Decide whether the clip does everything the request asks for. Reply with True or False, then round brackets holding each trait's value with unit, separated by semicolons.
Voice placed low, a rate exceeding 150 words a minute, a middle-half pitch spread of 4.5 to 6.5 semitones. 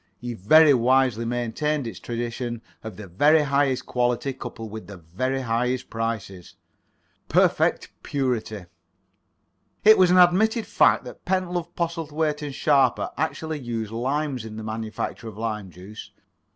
False (125 Hz; 140 wpm; 5.1 semitones)